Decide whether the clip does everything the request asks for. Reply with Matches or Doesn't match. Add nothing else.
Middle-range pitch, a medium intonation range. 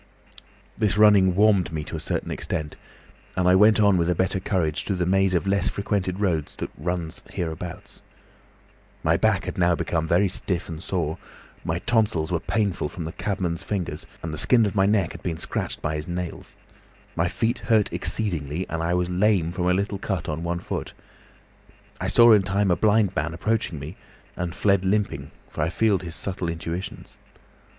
Doesn't match